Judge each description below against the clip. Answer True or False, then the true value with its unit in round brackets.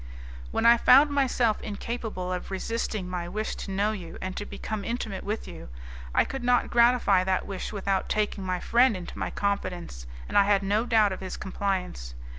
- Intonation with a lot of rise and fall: False (3.7 semitones)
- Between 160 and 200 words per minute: True (190 wpm)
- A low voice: False (200 Hz)